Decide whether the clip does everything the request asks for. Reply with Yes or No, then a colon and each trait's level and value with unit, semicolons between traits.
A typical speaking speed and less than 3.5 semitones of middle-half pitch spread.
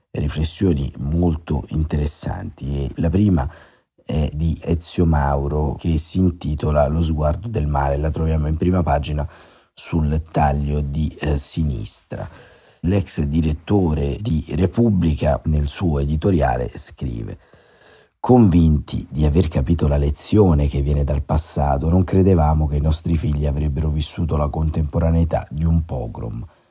Yes: average, 130 wpm; narrow, 2.5 semitones